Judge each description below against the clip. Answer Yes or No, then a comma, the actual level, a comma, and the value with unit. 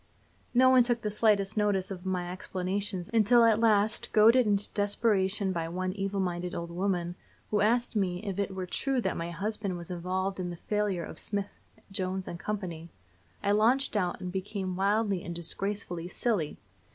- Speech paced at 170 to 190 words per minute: Yes, average, 175 wpm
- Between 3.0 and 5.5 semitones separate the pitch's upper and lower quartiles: No, narrow, 2.6 semitones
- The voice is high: Yes, high, 195 Hz